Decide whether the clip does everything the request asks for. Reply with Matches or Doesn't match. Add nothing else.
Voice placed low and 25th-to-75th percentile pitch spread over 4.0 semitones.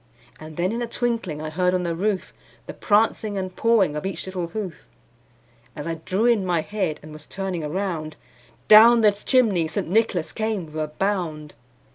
Doesn't match